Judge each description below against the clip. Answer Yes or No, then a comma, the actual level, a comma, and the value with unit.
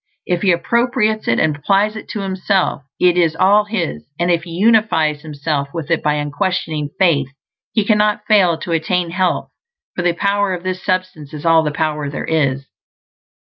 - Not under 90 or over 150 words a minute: No, average, 180 wpm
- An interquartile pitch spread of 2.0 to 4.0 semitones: No, average, 4.4 semitones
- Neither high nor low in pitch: Yes, medium, 175 Hz